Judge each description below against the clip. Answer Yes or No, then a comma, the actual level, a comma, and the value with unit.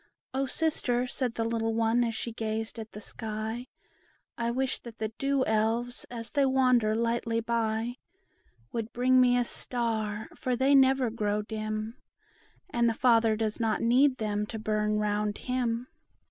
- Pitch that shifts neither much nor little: No, narrow, 2.2 semitones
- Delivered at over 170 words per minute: No, average, 160 wpm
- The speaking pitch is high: Yes, high, 230 Hz